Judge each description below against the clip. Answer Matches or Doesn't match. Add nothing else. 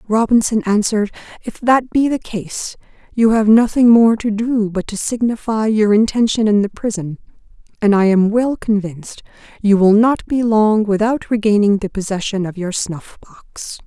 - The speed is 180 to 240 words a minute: Doesn't match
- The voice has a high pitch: Matches